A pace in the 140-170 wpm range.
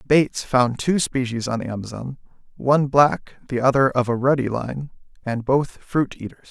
Yes: average, 165 wpm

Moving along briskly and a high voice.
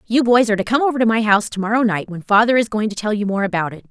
Yes: fast, 320 wpm; high, 215 Hz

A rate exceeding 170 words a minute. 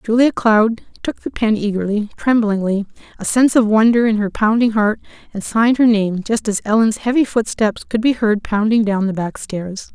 Yes: average, 195 wpm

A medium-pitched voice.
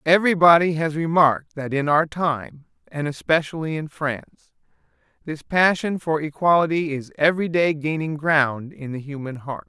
Yes: medium, 155 Hz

